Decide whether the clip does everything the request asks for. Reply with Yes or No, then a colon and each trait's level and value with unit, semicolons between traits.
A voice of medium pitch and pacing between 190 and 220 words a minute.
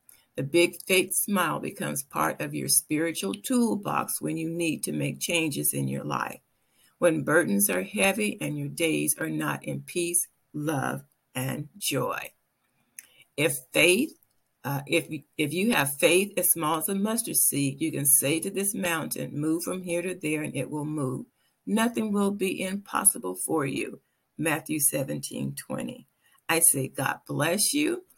No: medium, 160 Hz; average, 160 wpm